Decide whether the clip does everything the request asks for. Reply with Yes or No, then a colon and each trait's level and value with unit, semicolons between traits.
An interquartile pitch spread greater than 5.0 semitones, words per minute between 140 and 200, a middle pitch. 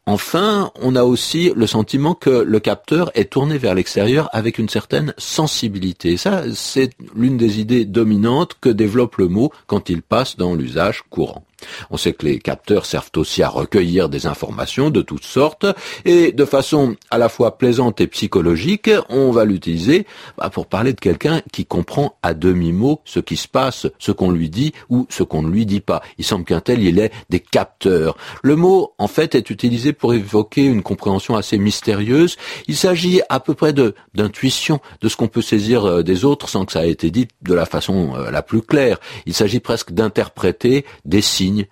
No: wide, 5.5 semitones; average, 195 wpm; low, 115 Hz